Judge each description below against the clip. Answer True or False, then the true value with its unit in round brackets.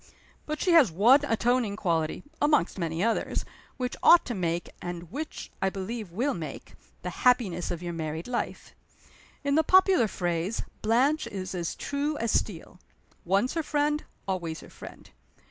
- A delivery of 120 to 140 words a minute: False (160 wpm)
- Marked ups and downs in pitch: True (8.3 semitones)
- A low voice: False (210 Hz)